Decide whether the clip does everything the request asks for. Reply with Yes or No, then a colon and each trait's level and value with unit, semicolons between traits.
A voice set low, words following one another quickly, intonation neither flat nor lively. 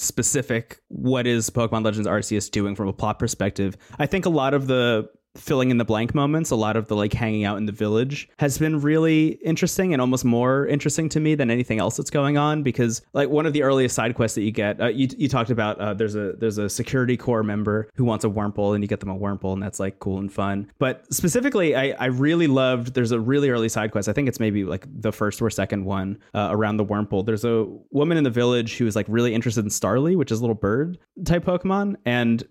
Yes: low, 115 Hz; fast, 250 wpm; average, 4.8 semitones